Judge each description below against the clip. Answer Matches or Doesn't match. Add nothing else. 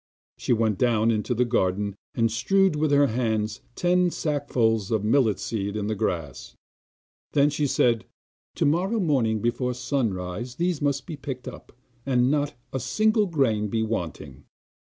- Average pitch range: Matches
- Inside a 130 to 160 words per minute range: Matches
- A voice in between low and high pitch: Doesn't match